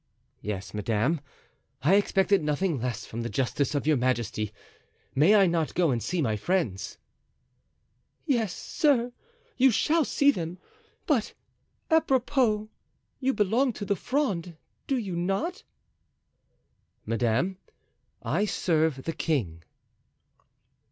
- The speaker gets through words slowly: Yes, slow, 120 wpm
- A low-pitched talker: No, medium, 175 Hz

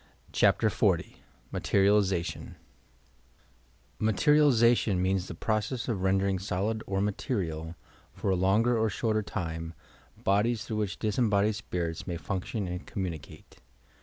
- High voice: No, low, 100 Hz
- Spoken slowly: Yes, slow, 120 wpm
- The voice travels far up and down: No, average, 3.1 semitones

